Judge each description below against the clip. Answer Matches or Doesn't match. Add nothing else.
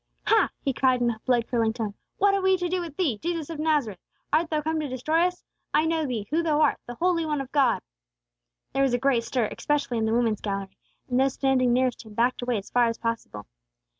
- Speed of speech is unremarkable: Doesn't match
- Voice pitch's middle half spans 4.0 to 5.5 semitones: Matches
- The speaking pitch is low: Doesn't match